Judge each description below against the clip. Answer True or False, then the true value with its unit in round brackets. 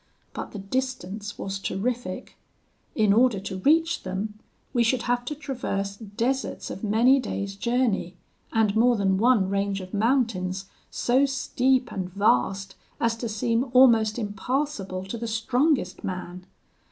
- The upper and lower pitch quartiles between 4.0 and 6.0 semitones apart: True (4.3 semitones)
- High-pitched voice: True (220 Hz)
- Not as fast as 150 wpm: True (140 wpm)